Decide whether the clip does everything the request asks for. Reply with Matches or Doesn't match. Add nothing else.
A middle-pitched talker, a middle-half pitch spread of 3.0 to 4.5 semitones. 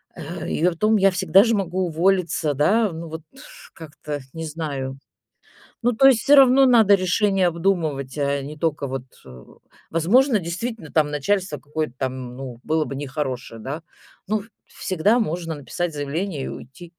Doesn't match